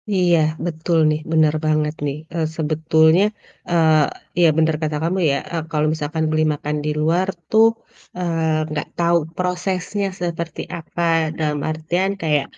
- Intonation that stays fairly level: Yes, narrow, 1.9 semitones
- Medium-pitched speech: Yes, medium, 160 Hz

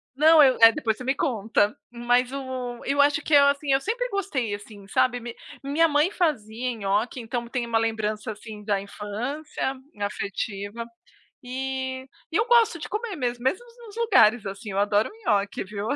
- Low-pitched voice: No, high, 245 Hz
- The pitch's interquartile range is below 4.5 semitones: No, average, 5.0 semitones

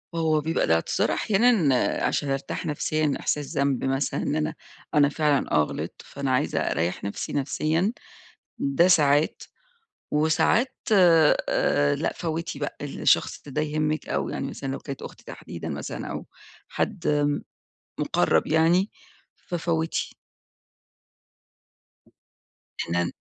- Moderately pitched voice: Yes, medium, 150 Hz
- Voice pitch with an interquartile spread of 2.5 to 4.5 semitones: Yes, average, 2.8 semitones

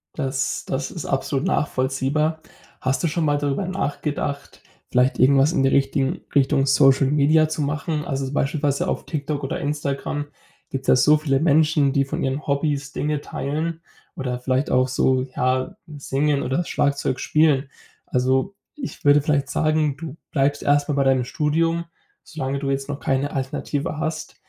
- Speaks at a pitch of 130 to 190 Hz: Yes, medium, 140 Hz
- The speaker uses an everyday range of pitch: No, narrow, 2.1 semitones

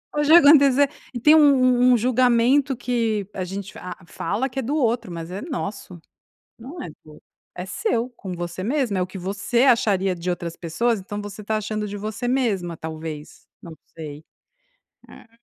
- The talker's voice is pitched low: No, high, 215 Hz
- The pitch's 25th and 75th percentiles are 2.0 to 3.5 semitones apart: No, wide, 5.6 semitones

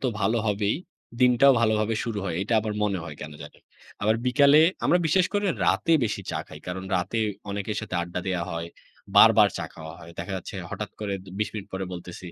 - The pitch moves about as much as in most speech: Yes, average, 4.4 semitones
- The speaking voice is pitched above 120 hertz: No, low, 105 Hz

